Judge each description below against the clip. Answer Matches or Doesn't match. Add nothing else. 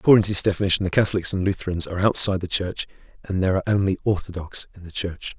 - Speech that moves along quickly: Matches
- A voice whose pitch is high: Doesn't match